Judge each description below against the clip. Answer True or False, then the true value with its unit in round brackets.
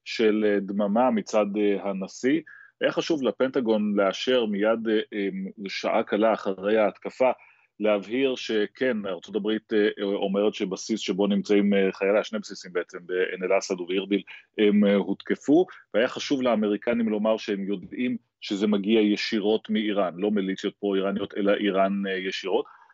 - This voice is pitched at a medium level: False (105 Hz)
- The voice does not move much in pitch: True (1.7 semitones)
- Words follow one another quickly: False (120 wpm)